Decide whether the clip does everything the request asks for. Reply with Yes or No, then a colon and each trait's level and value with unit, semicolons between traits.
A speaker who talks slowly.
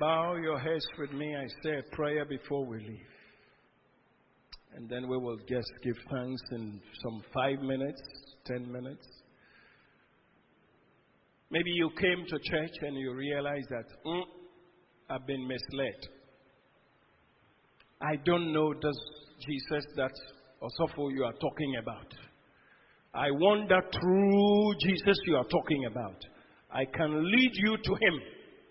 Yes: slow, 130 wpm